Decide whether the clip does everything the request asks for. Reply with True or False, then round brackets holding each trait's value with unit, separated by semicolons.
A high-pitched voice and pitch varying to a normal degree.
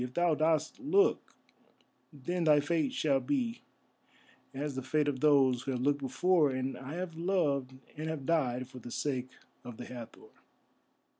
False (145 Hz; 4.1 semitones)